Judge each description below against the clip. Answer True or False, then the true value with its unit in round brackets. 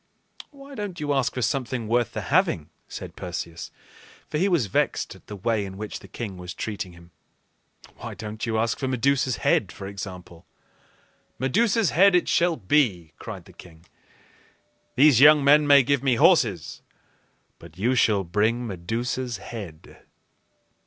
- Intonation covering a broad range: True (6.5 semitones)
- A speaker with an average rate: True (160 wpm)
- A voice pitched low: True (115 Hz)